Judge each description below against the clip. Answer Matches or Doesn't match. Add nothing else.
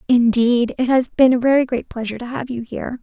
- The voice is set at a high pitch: Matches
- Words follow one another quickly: Matches